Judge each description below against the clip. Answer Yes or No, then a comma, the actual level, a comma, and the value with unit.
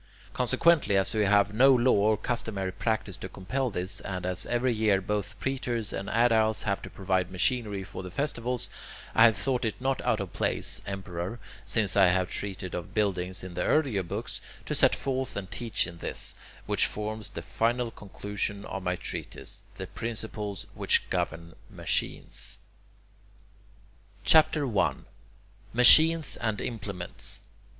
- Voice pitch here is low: Yes, low, 105 Hz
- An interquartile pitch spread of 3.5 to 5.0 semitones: Yes, average, 3.8 semitones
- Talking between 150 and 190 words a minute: Yes, average, 155 wpm